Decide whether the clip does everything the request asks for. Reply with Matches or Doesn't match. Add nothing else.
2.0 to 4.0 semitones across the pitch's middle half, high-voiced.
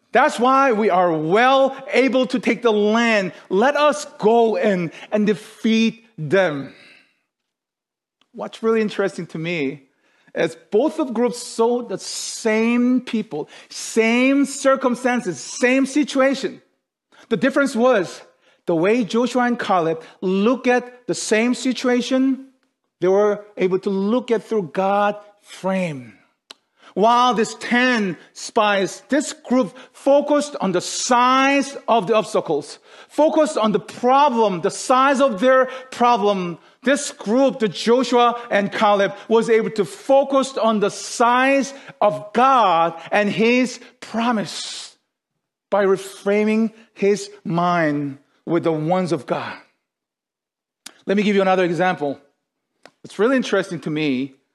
Doesn't match